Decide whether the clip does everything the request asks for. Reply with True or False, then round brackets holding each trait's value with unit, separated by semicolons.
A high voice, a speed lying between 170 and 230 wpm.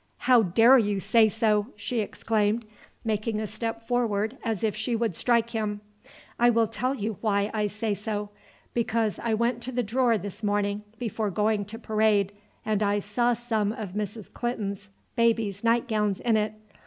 True (220 Hz; 175 wpm)